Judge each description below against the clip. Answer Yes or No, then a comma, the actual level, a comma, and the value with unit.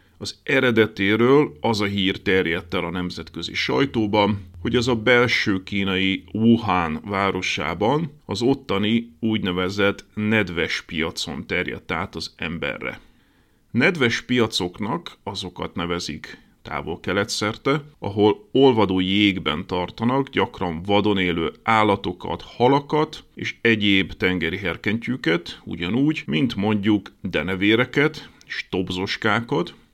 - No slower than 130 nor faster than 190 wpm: No, slow, 105 wpm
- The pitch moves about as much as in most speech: Yes, average, 3.8 semitones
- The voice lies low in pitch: Yes, low, 105 Hz